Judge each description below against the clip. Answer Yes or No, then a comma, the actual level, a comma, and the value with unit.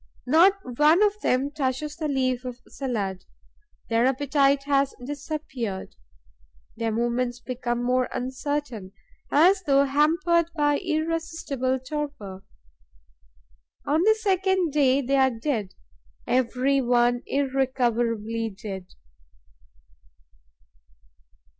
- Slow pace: Yes, slow, 95 wpm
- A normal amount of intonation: Yes, average, 3.8 semitones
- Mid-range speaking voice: No, very high, 270 Hz